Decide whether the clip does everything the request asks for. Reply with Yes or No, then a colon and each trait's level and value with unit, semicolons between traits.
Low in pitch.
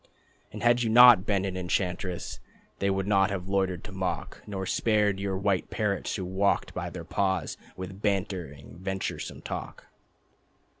Yes: very low, 95 Hz